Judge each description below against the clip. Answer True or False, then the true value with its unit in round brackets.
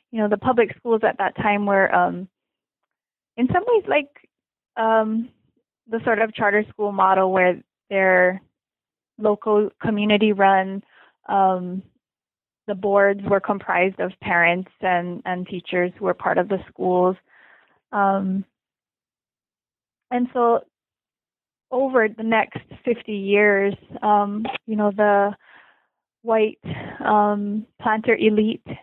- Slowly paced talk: True (120 wpm)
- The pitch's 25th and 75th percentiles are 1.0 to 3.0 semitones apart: True (2.6 semitones)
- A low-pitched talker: False (210 Hz)